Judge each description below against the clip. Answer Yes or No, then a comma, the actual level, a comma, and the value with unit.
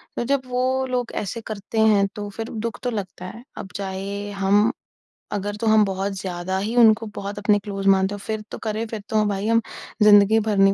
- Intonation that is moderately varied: No, narrow, 2.3 semitones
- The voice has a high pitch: Yes, high, 205 Hz